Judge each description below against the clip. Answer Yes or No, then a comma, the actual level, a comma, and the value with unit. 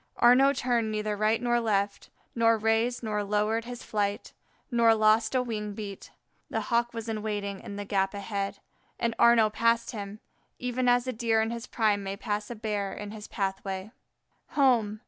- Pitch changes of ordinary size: No, narrow, 2.3 semitones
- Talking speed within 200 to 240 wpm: No, average, 185 wpm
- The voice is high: Yes, high, 220 Hz